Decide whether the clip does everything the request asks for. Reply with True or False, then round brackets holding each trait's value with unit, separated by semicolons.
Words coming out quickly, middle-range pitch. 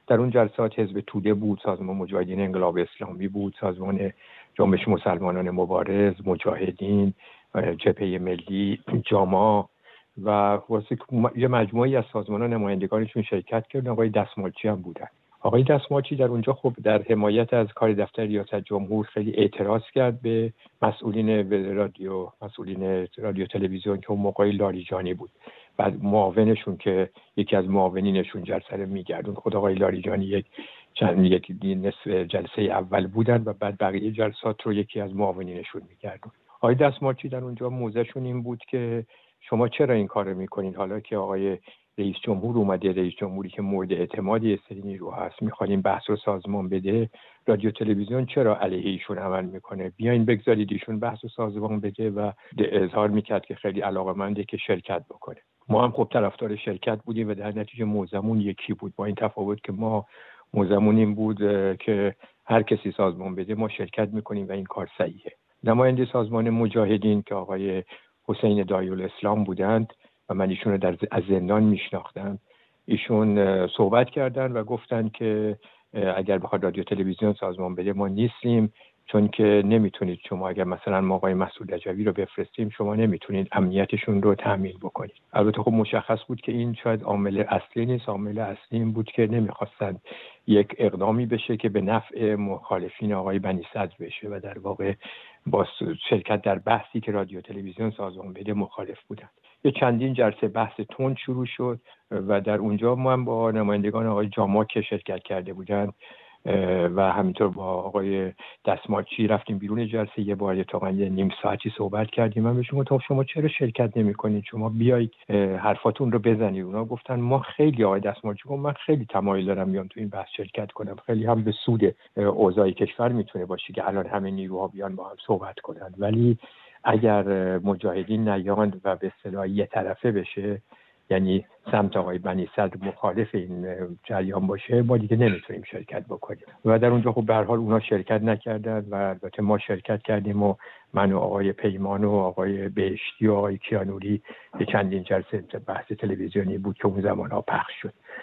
False (165 wpm; 105 Hz)